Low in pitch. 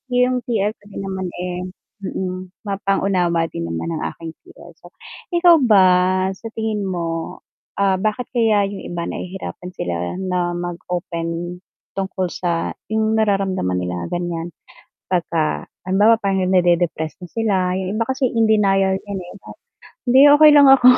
No: high, 190 Hz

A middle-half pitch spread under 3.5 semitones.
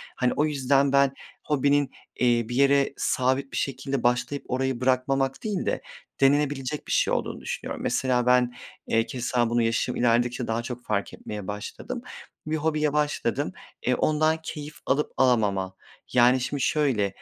Yes: average, 2.8 semitones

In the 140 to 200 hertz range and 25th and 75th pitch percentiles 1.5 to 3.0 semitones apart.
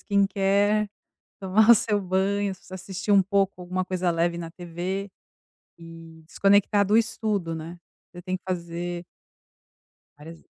Yes: medium, 185 Hz; narrow, 2.6 semitones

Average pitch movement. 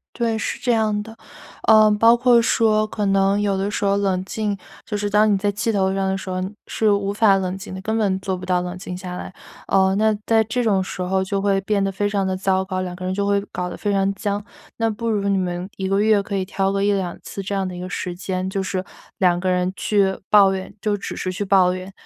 No: narrow, 1.7 semitones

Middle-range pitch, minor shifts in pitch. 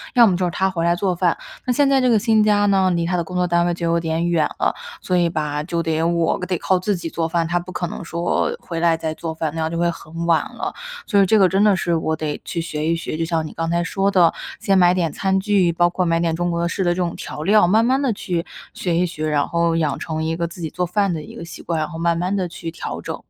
Yes: medium, 170 Hz; narrow, 2.1 semitones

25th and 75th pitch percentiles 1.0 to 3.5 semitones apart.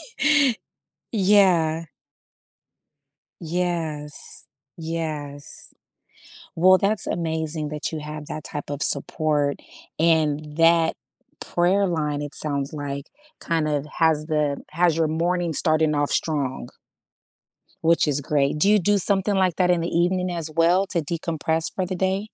Yes: average, 2.9 semitones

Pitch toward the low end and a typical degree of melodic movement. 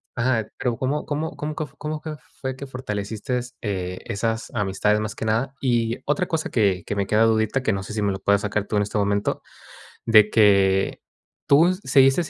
Yes: low, 110 Hz; average, 4.5 semitones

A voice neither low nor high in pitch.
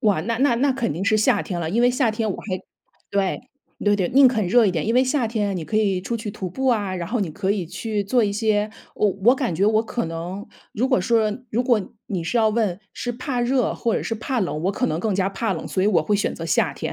No: high, 210 Hz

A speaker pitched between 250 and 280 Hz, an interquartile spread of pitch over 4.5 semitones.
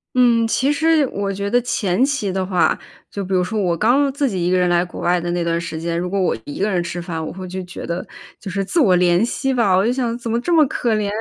No: high, 195 Hz; average, 5.2 semitones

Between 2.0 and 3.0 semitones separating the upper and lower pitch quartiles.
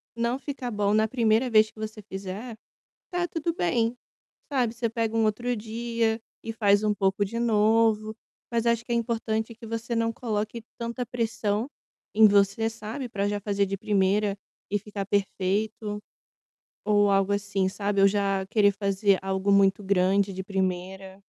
Yes: narrow, 2.5 semitones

